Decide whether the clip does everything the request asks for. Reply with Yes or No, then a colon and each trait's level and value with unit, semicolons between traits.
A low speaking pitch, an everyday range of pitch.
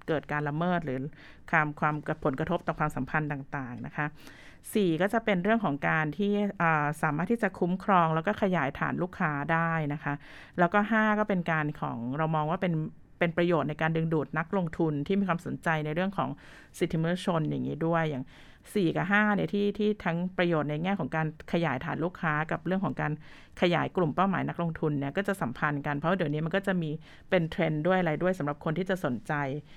No: medium, 165 Hz; average, 3.5 semitones